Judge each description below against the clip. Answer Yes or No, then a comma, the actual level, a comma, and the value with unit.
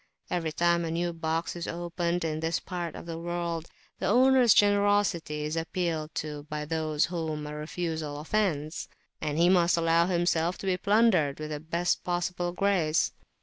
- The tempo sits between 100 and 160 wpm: No, average, 170 wpm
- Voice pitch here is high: No, medium, 170 Hz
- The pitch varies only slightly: Yes, narrow, 2.1 semitones